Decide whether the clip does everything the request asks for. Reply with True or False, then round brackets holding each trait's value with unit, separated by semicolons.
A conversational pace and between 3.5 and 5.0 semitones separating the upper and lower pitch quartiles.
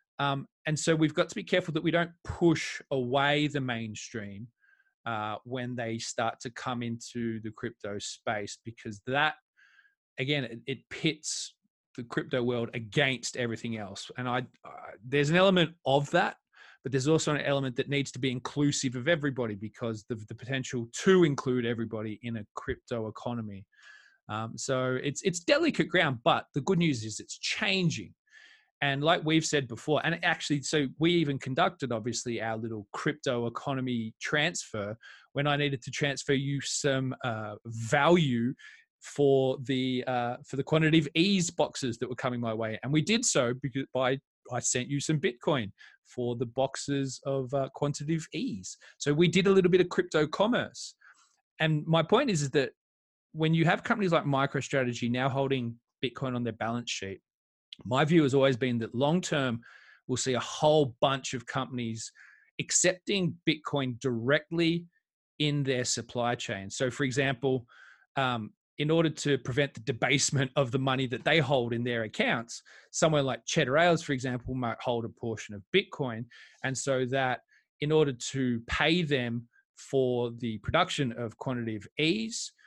True (170 wpm; 4.5 semitones)